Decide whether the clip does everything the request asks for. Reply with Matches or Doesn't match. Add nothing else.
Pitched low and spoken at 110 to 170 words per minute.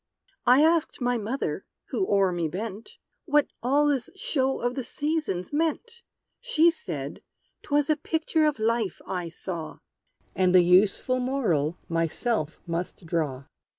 Doesn't match